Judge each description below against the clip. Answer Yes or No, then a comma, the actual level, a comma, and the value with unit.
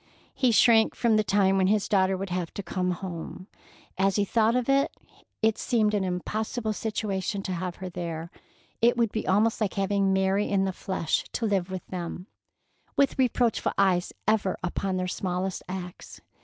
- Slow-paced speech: No, average, 180 wpm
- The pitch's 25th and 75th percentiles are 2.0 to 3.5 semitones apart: Yes, average, 2.8 semitones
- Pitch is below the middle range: No, high, 195 Hz